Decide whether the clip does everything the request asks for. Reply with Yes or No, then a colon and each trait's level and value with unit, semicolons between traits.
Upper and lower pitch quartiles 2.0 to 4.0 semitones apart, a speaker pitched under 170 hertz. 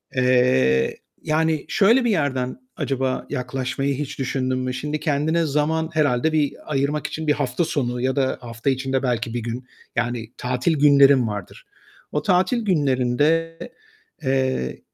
Yes: average, 3.4 semitones; low, 135 Hz